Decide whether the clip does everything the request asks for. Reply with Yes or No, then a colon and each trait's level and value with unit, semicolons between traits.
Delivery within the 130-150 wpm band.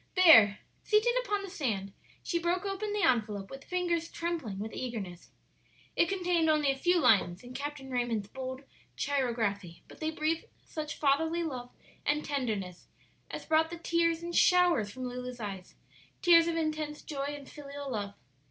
No: average, 160 wpm